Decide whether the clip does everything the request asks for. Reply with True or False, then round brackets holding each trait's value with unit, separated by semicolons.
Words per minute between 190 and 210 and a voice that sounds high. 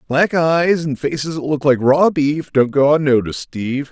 False (200 wpm; 145 Hz)